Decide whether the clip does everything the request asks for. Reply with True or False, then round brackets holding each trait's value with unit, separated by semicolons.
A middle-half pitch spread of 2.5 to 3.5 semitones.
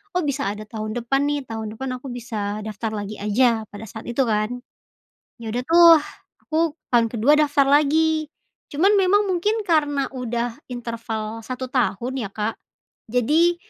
False (5.0 semitones)